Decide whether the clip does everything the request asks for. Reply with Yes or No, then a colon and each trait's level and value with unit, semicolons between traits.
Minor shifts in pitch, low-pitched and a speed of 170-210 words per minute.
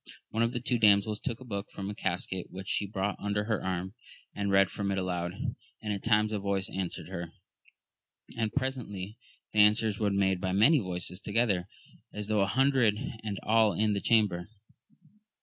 Yes: narrow, 2.3 semitones; low, 100 Hz; average, 185 wpm